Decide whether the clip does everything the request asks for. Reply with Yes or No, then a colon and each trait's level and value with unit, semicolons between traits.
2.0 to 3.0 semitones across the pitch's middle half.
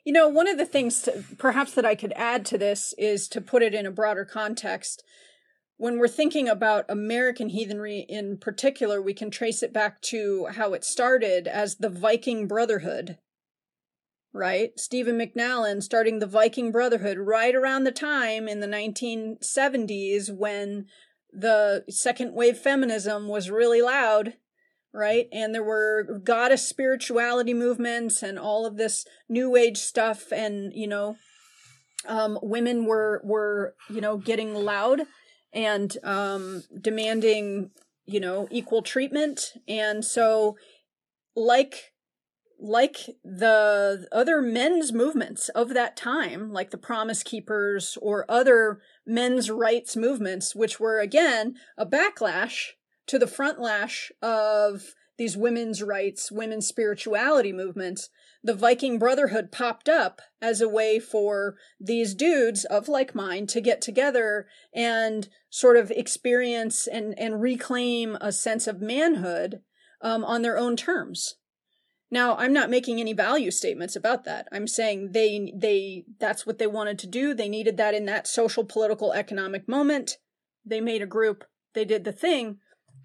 Yes: narrow, 2.6 semitones